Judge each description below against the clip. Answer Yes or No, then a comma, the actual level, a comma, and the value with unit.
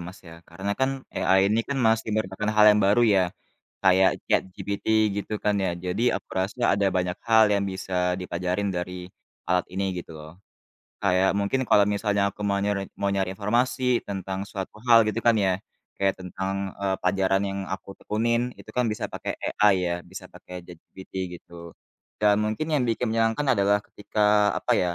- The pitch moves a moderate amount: No, narrow, 2.3 semitones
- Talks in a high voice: No, low, 100 Hz